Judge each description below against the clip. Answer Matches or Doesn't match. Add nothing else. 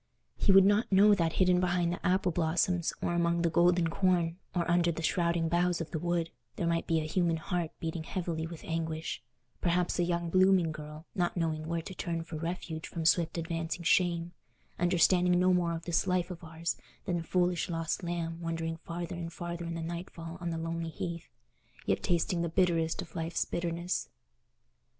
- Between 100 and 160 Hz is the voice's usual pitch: Doesn't match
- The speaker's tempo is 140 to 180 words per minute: Doesn't match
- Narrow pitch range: Matches